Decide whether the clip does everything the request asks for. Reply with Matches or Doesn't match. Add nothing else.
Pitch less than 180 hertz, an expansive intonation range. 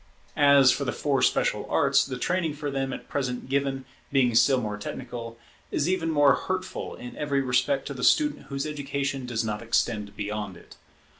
Doesn't match